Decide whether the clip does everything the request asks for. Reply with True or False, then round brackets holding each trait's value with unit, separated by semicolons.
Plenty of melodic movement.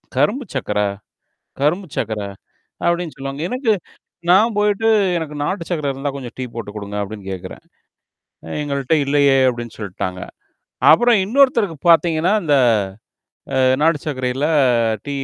True (6.5 semitones)